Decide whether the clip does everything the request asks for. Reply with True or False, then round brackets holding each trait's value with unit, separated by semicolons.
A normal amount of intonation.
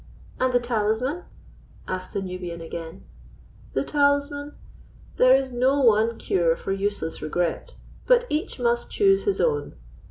False (7.5 semitones)